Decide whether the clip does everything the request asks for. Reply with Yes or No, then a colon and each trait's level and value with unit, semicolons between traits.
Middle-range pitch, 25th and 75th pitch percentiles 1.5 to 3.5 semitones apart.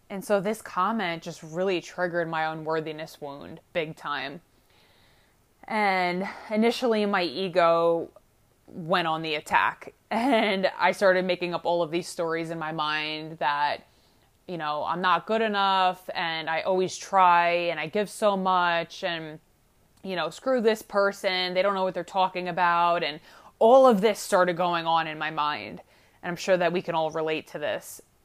Yes: medium, 175 Hz; average, 3.0 semitones